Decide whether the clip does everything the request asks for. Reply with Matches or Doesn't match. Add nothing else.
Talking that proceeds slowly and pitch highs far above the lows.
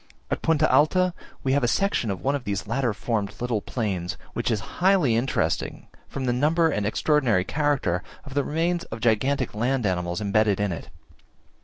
Doesn't match